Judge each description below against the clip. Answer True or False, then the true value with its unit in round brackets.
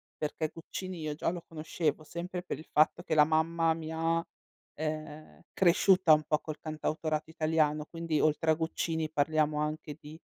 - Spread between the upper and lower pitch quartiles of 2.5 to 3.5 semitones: False (1.3 semitones)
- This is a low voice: False (155 Hz)